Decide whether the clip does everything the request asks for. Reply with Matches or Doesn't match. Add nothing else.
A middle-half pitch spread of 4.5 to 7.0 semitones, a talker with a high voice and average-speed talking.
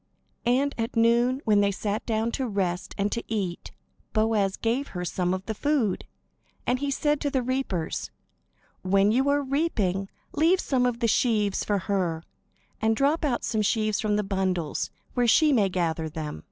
Matches